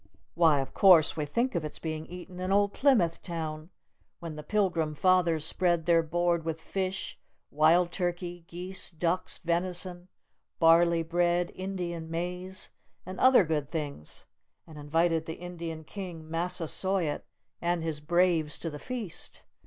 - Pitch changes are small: Yes, narrow, 2.0 semitones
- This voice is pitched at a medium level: Yes, medium, 170 Hz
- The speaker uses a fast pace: No, average, 145 wpm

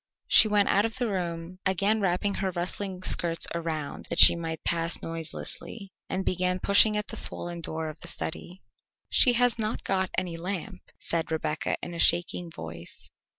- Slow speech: No, average, 175 wpm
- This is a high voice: No, medium, 180 Hz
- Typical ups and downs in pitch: Yes, average, 3.2 semitones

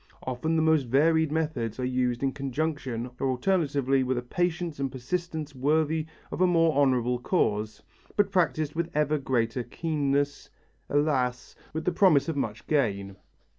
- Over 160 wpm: No, average, 155 wpm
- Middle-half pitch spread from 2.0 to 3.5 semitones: No, average, 4.0 semitones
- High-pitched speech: No, medium, 145 Hz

